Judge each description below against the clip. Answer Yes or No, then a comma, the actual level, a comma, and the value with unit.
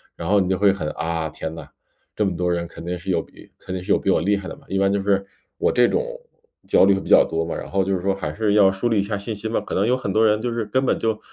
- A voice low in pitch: Yes, low, 100 Hz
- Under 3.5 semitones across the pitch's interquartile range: Yes, average, 2.8 semitones